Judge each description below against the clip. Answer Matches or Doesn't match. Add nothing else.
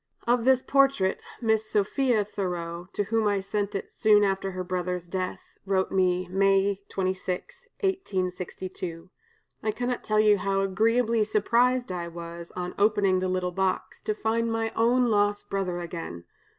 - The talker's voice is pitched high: Matches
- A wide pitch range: Doesn't match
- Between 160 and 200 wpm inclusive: Doesn't match